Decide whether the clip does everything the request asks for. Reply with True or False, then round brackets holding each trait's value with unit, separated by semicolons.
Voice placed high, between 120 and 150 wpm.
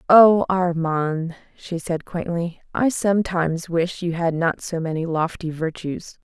False (170 Hz; 145 wpm)